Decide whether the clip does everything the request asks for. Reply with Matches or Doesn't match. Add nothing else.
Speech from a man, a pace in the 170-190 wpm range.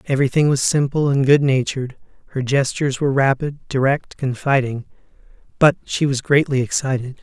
Doesn't match